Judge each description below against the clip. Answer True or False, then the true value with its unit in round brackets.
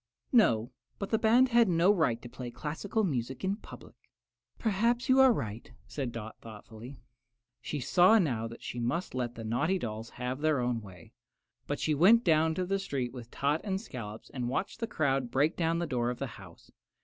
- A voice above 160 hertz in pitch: False (140 Hz)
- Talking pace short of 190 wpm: False (195 wpm)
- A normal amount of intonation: False (8.1 semitones)